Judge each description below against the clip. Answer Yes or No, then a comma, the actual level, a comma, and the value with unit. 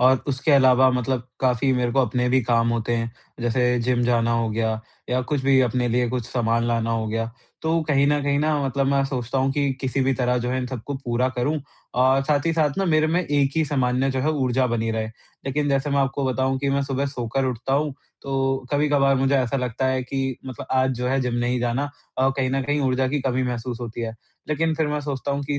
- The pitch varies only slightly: Yes, narrow, 2.2 semitones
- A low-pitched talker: Yes, low, 130 Hz